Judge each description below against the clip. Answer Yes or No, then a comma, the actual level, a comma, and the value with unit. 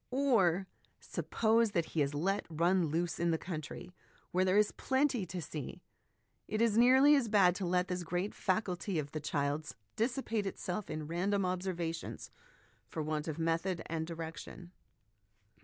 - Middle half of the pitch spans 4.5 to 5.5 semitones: No, average, 4.1 semitones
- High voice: No, medium, 180 Hz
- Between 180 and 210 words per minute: No, average, 155 wpm